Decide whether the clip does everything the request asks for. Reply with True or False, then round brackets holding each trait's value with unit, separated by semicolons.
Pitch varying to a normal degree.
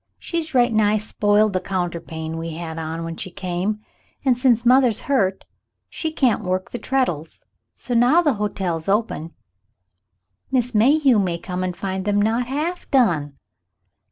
False (6.0 semitones)